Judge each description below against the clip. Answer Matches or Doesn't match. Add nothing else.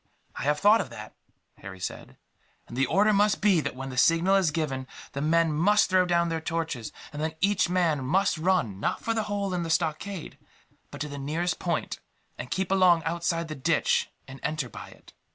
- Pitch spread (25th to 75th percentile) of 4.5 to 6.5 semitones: Doesn't match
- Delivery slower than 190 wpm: Doesn't match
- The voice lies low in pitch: Doesn't match